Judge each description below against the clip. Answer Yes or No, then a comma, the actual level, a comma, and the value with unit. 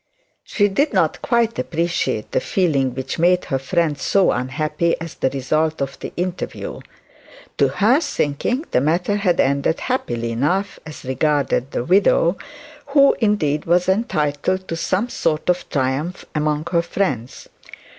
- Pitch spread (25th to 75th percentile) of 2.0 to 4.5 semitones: No, average, 5.3 semitones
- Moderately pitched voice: Yes, medium, 165 Hz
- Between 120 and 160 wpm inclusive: Yes, average, 145 wpm